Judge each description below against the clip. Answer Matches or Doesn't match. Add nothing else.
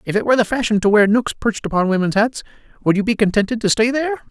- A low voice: Doesn't match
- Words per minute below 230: Doesn't match